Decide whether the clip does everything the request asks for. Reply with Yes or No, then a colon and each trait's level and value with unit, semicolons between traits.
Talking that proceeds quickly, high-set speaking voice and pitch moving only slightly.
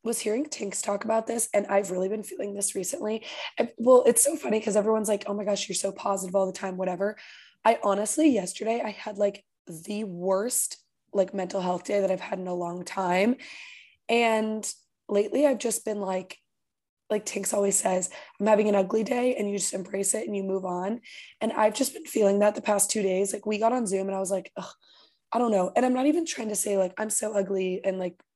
Yes: fast, 230 wpm; high, 205 Hz; narrow, 2.3 semitones